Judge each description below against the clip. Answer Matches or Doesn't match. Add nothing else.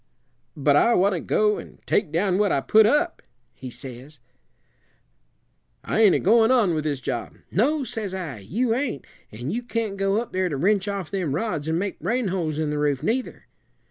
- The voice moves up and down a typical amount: Doesn't match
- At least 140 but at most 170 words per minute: Doesn't match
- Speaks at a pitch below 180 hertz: Doesn't match